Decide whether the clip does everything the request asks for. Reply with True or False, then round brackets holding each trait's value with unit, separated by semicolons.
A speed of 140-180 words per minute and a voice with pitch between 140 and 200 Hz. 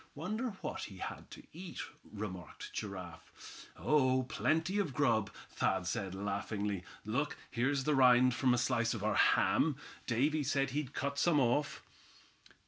False (145 wpm; 130 Hz)